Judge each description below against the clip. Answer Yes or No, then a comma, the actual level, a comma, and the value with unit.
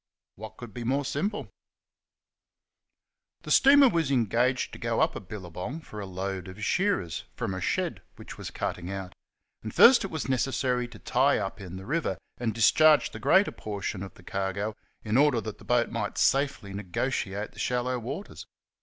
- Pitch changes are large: Yes, wide, 5.7 semitones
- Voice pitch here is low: Yes, low, 115 Hz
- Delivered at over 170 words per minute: Yes, average, 180 wpm